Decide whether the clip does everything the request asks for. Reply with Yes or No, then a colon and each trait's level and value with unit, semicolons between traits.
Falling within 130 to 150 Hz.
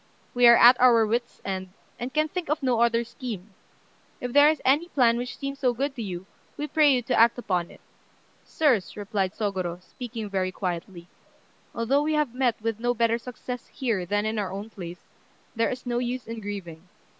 No: high, 235 Hz